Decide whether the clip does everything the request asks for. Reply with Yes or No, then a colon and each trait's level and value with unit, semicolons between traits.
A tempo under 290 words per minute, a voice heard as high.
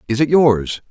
No: average, 200 wpm; low, 125 Hz